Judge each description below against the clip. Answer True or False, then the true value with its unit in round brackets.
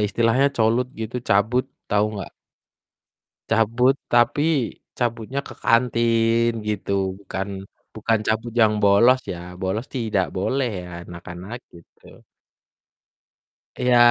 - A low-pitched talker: True (115 Hz)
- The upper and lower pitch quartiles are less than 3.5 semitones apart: True (2.9 semitones)